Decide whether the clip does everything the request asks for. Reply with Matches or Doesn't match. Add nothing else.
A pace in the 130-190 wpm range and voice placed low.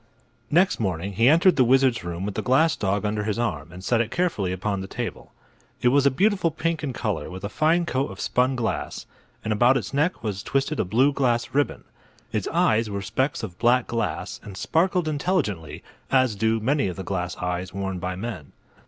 Doesn't match